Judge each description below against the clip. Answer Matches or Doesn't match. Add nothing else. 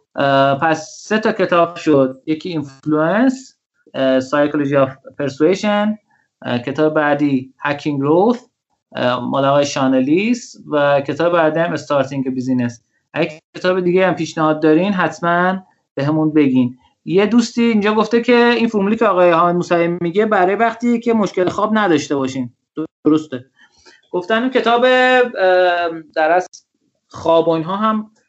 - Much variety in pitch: Matches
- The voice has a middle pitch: Matches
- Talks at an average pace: Matches